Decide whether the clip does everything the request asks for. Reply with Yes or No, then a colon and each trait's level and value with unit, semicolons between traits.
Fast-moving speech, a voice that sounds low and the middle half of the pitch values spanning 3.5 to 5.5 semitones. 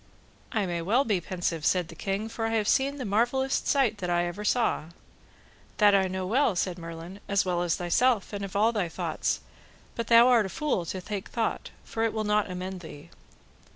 No: fast, 215 wpm; high, 200 Hz; average, 4.0 semitones